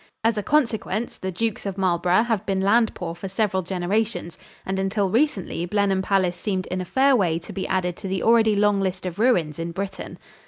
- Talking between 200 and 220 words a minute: Yes, fast, 205 wpm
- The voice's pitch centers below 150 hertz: No, high, 195 Hz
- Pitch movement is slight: No, average, 3.1 semitones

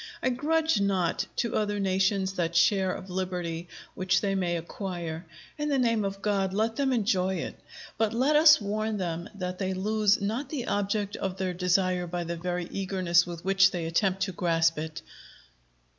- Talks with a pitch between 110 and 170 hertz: No, high, 190 Hz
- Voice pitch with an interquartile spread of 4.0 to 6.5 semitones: No, average, 2.9 semitones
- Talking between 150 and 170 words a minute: No, average, 180 wpm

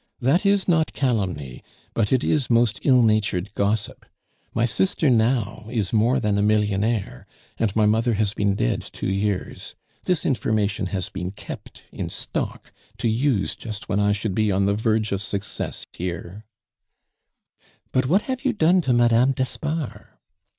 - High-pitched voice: No, low, 110 Hz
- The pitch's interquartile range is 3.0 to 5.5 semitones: Yes, average, 4.1 semitones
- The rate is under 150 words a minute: No, average, 165 wpm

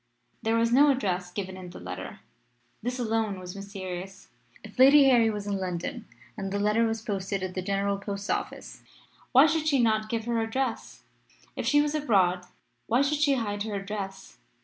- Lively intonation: No, average, 3.9 semitones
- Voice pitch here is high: Yes, high, 215 Hz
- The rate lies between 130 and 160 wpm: No, average, 185 wpm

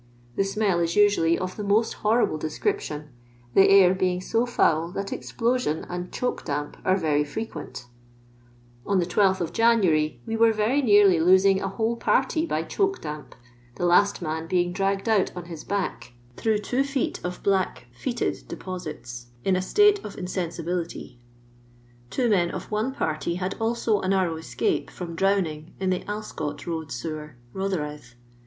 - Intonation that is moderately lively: Yes, average, 4.6 semitones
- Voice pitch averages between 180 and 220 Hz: Yes, medium, 185 Hz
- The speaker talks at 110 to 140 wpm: No, average, 160 wpm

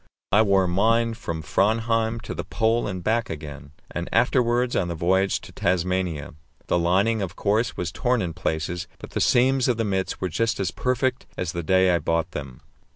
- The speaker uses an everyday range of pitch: Yes, average, 4.9 semitones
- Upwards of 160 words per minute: Yes, average, 195 wpm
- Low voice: Yes, very low, 95 Hz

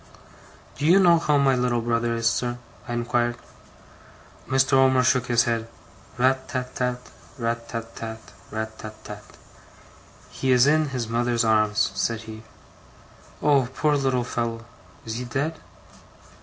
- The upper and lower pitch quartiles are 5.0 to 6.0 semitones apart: No, narrow, 2.4 semitones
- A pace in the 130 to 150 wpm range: Yes, average, 145 wpm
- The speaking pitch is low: Yes, low, 120 Hz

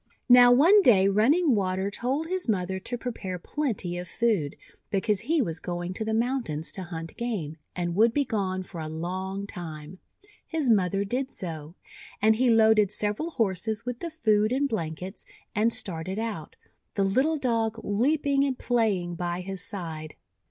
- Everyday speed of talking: Yes, average, 165 wpm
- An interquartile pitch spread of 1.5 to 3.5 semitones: No, average, 5.2 semitones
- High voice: Yes, high, 210 Hz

